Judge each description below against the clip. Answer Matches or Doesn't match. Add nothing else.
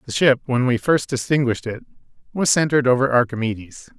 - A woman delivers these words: Doesn't match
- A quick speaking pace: Doesn't match